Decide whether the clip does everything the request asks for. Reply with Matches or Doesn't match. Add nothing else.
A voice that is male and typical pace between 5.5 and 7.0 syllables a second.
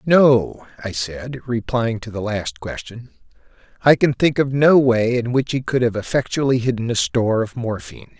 Doesn't match